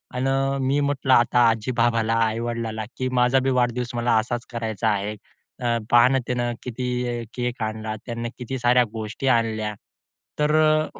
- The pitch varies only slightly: Yes, narrow, 2.2 semitones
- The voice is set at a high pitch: No, low, 120 Hz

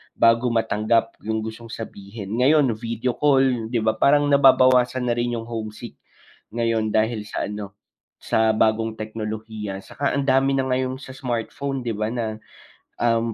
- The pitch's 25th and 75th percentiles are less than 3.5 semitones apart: Yes, narrow, 2.6 semitones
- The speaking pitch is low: Yes, low, 115 Hz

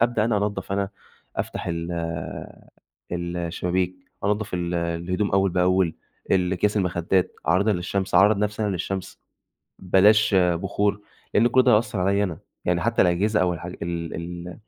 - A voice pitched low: Yes, very low, 95 Hz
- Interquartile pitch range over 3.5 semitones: No, average, 2.8 semitones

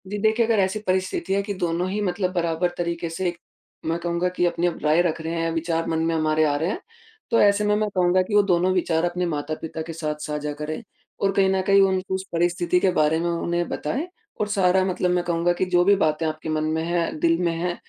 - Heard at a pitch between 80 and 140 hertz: No, medium, 175 Hz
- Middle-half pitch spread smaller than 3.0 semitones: Yes, narrow, 2.4 semitones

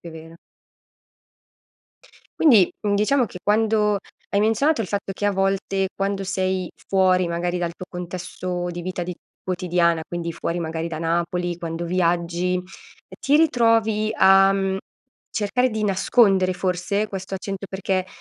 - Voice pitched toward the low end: No, high, 190 Hz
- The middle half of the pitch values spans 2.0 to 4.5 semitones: Yes, average, 2.7 semitones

